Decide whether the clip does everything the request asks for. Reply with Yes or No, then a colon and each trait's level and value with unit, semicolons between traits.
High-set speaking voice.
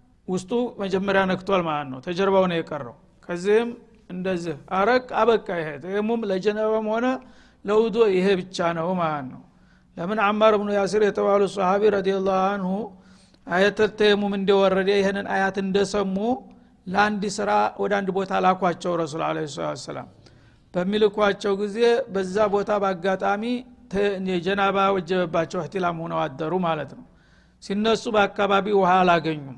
Yes: high, 195 Hz